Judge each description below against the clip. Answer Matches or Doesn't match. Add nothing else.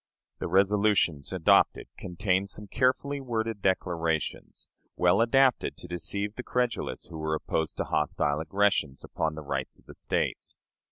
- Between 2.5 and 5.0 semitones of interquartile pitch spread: Doesn't match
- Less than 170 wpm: Matches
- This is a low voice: Matches